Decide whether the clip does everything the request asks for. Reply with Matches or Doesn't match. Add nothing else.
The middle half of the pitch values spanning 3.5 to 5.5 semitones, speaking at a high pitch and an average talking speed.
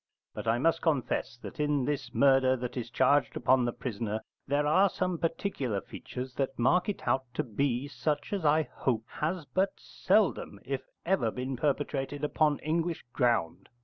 Doesn't match